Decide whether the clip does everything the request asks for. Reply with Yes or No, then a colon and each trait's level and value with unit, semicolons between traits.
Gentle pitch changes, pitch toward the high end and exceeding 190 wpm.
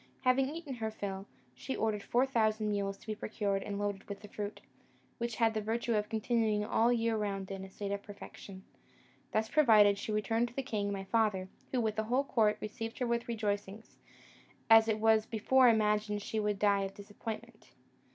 Yes: narrow, 2.0 semitones; high, 215 Hz; average, 200 wpm